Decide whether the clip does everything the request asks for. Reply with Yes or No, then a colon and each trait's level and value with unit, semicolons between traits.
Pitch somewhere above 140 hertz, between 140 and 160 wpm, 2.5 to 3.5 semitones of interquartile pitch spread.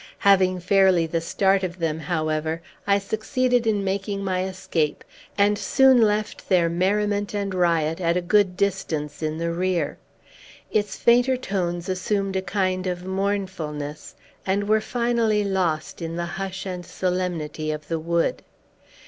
Yes: medium, 185 Hz; average, 150 wpm; average, 3.1 semitones